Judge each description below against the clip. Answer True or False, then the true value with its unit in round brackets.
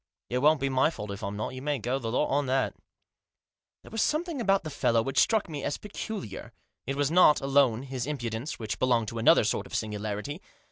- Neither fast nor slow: False (220 wpm)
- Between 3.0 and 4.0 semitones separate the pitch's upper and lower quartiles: False (4.6 semitones)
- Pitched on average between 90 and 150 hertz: True (135 Hz)